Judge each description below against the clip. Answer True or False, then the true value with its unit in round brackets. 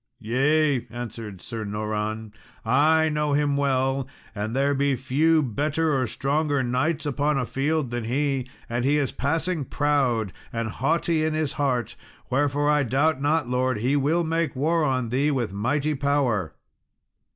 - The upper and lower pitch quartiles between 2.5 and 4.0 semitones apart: True (3.6 semitones)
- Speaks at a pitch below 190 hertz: True (140 Hz)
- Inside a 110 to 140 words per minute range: False (155 wpm)